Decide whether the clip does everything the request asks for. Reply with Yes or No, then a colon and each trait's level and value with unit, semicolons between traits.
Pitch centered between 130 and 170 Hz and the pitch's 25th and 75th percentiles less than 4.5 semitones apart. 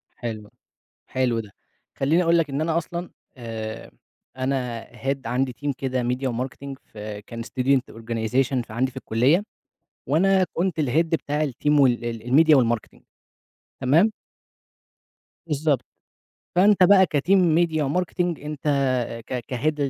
No: low, 135 Hz; average, 4.8 semitones